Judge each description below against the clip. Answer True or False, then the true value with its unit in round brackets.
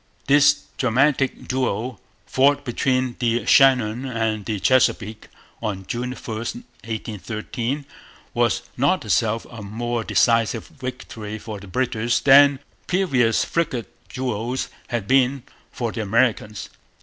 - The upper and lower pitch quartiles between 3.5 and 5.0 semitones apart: False (3.1 semitones)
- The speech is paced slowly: True (115 wpm)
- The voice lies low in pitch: True (120 Hz)